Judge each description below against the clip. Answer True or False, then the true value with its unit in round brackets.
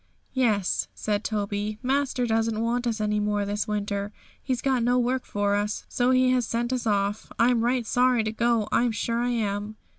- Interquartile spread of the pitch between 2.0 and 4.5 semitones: True (2.9 semitones)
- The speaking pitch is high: True (225 Hz)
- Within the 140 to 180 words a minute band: False (190 wpm)